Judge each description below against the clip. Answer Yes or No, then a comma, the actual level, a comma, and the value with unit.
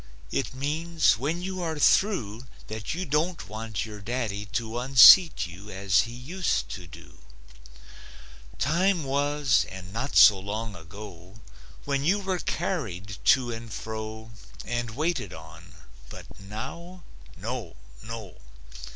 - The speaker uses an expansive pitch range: Yes, wide, 6.7 semitones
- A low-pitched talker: Yes, low, 115 Hz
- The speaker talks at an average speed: No, slow, 130 wpm